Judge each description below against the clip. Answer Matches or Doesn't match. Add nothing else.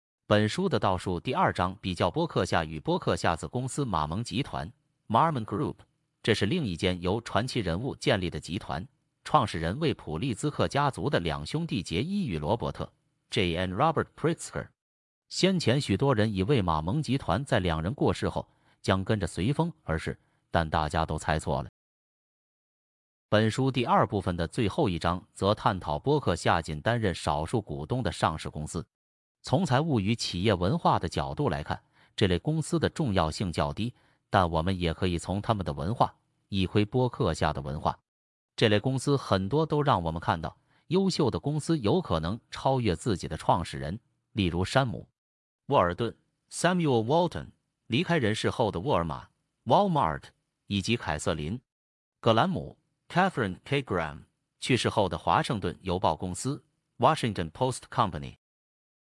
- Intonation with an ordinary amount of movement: Doesn't match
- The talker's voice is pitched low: Matches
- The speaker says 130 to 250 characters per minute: Doesn't match